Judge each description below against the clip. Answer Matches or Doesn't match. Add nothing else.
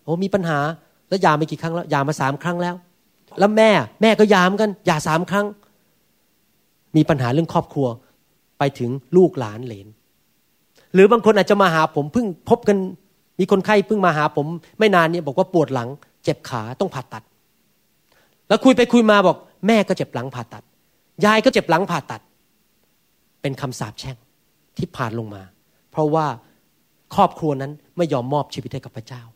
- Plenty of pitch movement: Matches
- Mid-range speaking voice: Matches